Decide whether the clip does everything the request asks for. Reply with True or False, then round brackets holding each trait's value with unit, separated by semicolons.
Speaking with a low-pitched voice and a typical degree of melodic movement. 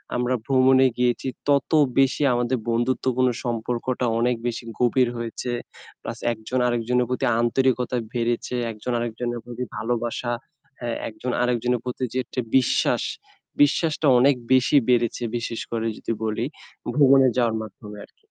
False (125 Hz; 1.6 semitones)